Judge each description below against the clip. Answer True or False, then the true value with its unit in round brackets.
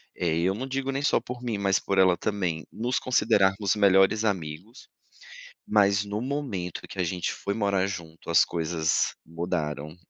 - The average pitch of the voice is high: False (95 Hz)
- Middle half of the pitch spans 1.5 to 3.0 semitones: False (3.9 semitones)